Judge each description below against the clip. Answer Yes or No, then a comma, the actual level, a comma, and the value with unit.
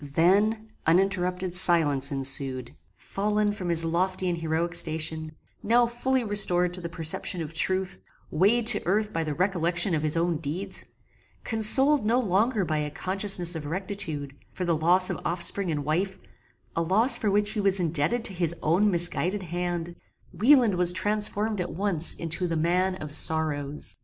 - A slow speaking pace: No, average, 165 wpm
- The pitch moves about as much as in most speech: Yes, average, 3.9 semitones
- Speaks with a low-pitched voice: No, medium, 180 Hz